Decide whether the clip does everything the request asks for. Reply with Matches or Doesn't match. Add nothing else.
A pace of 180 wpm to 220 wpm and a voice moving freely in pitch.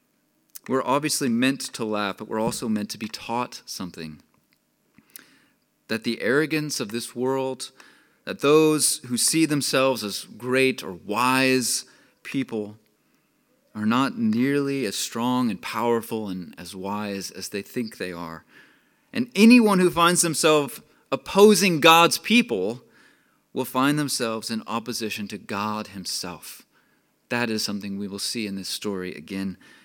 Doesn't match